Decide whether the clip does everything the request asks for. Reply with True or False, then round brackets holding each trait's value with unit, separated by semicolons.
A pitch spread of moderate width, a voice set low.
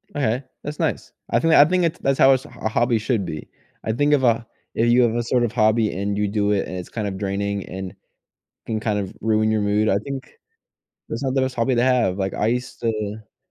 True (3.8 semitones; 110 Hz)